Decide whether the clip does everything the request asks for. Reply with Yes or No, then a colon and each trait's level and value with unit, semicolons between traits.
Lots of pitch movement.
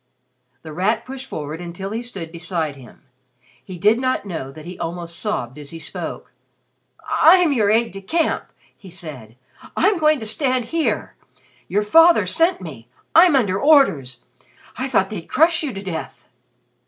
Yes: wide, 8.5 semitones